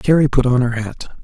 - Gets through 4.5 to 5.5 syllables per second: Yes, 5.2 syllables/s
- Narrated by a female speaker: No, male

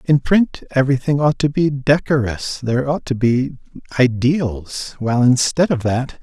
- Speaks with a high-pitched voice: No, low, 135 Hz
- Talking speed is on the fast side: No, average, 155 wpm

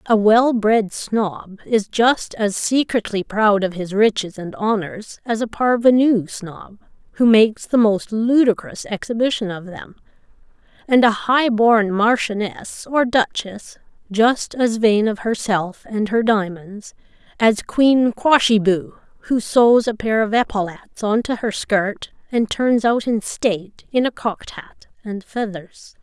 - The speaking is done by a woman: Yes, female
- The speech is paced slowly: No, average, 150 wpm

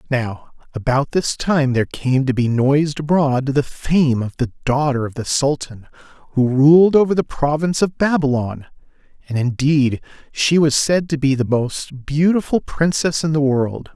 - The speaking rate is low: No, average, 170 wpm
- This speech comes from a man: Yes, male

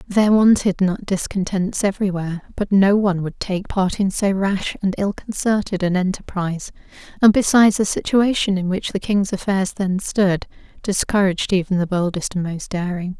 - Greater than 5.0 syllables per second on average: Yes, 5.2 syllables/s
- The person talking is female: Yes, female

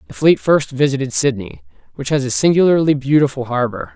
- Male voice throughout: Yes, male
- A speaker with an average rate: Yes, average, 165 wpm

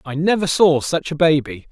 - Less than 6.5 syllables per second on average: Yes, 5.0 syllables/s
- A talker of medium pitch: Yes, medium, 155 Hz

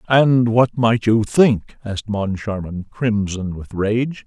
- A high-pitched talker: No, low, 110 Hz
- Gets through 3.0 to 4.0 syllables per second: Yes, 3.5 syllables/s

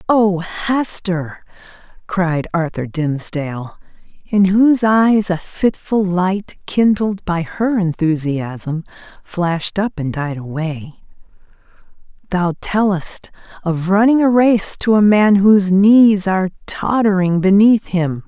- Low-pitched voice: No, high, 190 Hz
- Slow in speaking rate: Yes, slow, 115 wpm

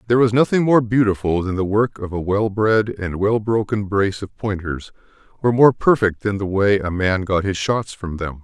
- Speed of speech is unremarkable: No, fast, 220 wpm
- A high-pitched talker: No, low, 105 Hz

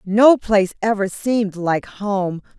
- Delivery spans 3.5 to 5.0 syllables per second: Yes, 4.0 syllables/s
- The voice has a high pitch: Yes, high, 205 Hz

